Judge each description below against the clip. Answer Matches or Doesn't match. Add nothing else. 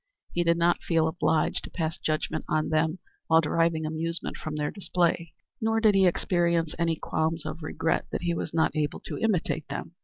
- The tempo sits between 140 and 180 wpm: Doesn't match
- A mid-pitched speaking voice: Matches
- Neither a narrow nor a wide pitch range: Doesn't match